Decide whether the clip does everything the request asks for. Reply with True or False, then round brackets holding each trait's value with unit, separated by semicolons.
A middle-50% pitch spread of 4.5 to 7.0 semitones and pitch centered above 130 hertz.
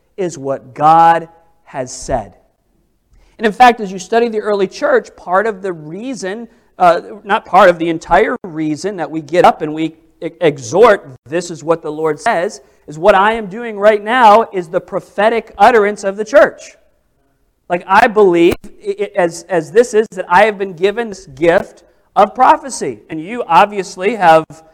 True (5.0 semitones; 190 Hz)